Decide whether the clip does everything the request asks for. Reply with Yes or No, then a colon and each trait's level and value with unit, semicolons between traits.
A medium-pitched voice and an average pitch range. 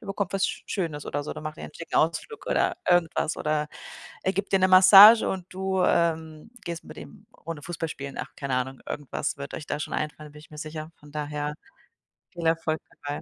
Yes: medium, 160 Hz; average, 3.8 semitones